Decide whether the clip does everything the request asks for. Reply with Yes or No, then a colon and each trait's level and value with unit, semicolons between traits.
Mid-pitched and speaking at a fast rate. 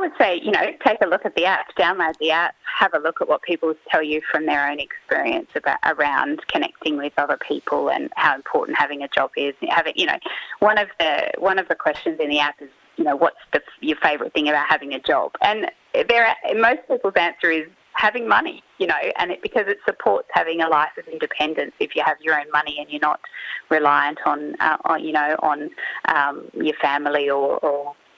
Yes: medium, 160 Hz; fast, 225 wpm